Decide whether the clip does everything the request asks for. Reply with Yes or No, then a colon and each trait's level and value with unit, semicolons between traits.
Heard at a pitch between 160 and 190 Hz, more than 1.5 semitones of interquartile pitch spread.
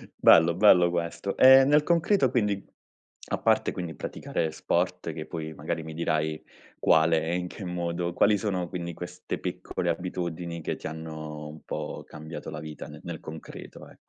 No: very low, 85 Hz; narrow, 2.4 semitones